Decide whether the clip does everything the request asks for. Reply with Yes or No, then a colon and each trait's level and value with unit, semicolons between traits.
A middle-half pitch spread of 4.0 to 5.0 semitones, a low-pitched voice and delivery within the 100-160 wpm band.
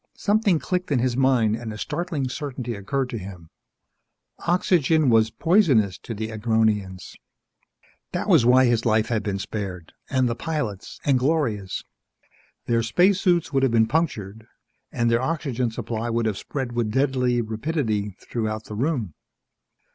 Yes: average, 4.3 semitones; low, 120 Hz; average, 150 wpm